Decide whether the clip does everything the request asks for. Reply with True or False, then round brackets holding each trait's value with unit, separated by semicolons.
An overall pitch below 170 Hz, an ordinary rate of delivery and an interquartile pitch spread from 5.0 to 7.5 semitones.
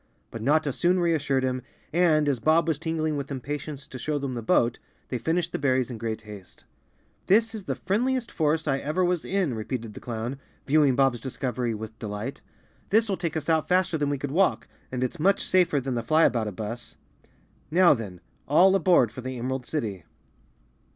True (140 Hz; 190 wpm; 5.4 semitones)